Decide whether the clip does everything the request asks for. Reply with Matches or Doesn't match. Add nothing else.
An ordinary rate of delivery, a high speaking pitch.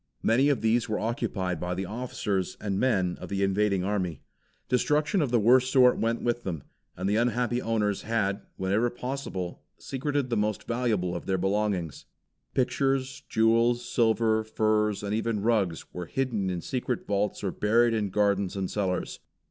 Doesn't match